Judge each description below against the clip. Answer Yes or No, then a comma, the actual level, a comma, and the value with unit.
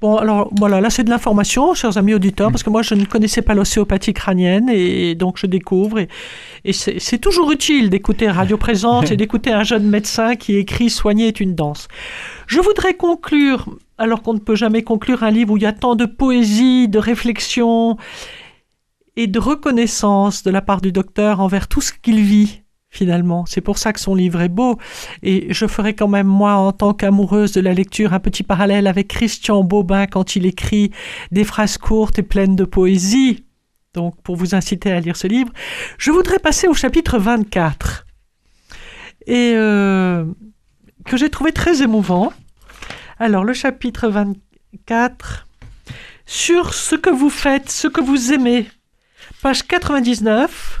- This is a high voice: Yes, high, 215 Hz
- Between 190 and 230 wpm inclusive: No, average, 175 wpm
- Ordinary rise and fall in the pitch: Yes, average, 3.7 semitones